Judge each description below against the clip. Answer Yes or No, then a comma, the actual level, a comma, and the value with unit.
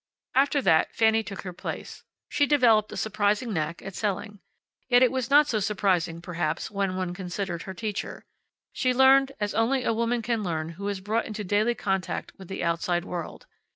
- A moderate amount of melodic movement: Yes, average, 4.2 semitones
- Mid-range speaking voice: No, high, 205 Hz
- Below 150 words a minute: No, average, 190 wpm